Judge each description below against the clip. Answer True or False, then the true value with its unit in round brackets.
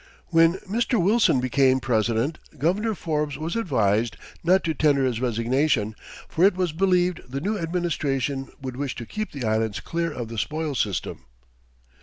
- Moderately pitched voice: True (145 Hz)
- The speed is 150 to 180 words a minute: True (160 wpm)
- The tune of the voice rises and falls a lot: True (6.0 semitones)